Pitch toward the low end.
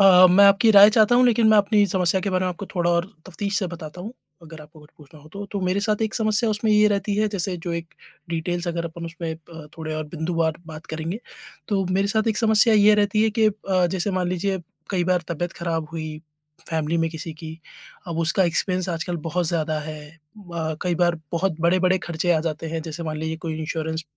No: medium, 175 Hz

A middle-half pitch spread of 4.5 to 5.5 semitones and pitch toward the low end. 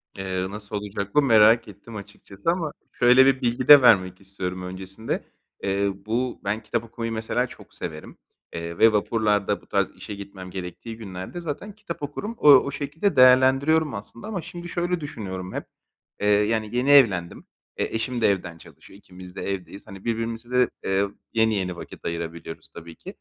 Yes: average, 5.1 semitones; low, 110 Hz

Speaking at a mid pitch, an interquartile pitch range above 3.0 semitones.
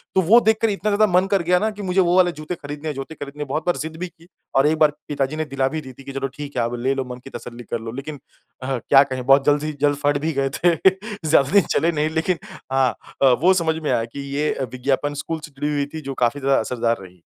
Yes: medium, 145 Hz; average, 3.8 semitones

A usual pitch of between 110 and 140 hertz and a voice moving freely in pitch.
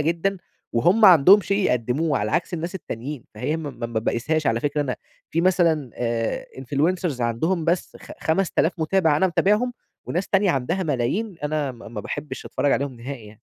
No: medium, 155 Hz; wide, 6.1 semitones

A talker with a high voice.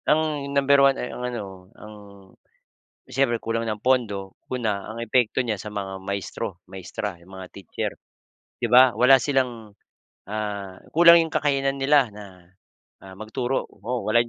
No: low, 115 Hz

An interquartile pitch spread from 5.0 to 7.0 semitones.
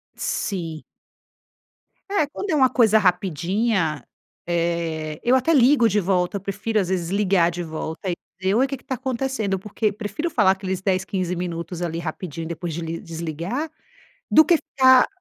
Yes: wide, 5.5 semitones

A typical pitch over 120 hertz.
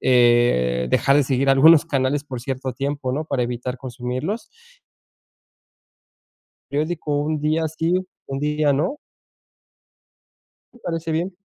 Yes: medium, 140 Hz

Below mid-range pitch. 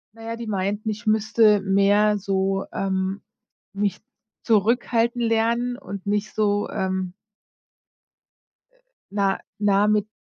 No: high, 205 Hz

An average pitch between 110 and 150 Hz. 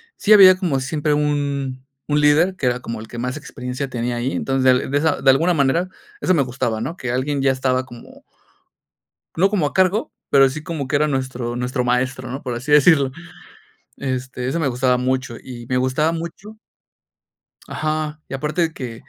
Yes: low, 135 Hz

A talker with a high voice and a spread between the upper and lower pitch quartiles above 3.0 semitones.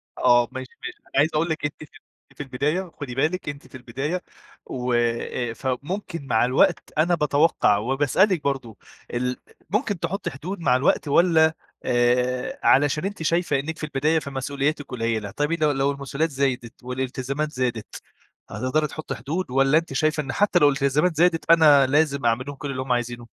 No: medium, 140 Hz; average, 3.7 semitones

